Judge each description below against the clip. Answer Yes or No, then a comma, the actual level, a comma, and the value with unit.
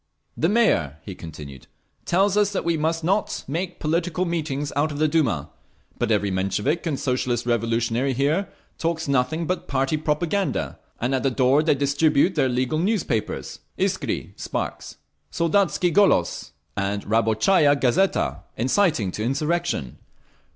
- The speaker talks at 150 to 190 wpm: No, average, 140 wpm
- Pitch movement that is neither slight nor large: No, wide, 6.1 semitones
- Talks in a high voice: No, medium, 145 Hz